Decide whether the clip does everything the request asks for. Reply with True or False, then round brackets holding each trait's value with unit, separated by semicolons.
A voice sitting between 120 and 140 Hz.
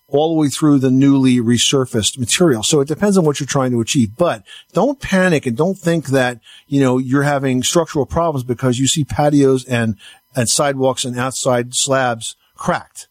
True (135 Hz)